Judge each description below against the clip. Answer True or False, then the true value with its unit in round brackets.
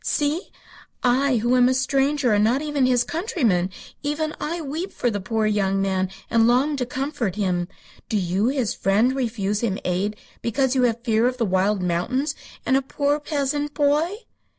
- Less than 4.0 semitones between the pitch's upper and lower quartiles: False (5.4 semitones)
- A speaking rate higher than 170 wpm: True (180 wpm)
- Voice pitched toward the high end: True (245 Hz)